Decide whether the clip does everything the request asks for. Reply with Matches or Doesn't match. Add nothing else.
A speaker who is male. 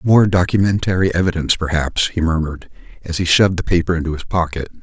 Matches